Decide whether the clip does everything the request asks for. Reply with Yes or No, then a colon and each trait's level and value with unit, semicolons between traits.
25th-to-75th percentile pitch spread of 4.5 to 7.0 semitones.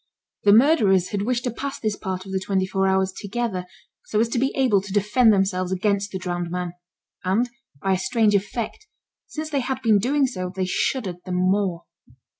No: average, 4.0 semitones